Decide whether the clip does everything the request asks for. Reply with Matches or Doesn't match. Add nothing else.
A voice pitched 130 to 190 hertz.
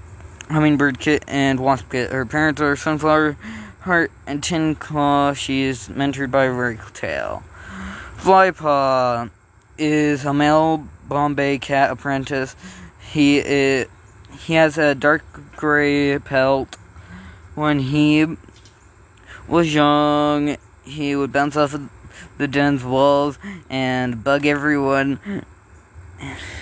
Matches